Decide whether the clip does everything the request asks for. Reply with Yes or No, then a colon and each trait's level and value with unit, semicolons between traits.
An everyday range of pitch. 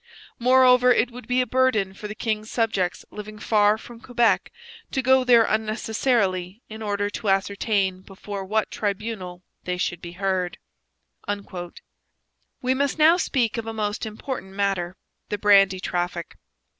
Yes: average, 3.7 semitones